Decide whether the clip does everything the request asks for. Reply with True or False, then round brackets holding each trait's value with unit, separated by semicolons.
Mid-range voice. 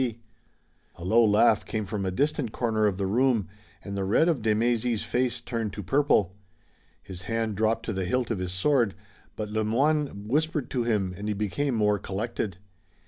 False (110 Hz)